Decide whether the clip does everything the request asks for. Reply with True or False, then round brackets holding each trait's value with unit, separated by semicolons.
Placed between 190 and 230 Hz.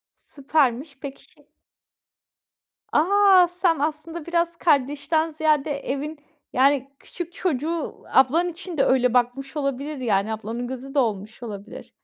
False (285 Hz)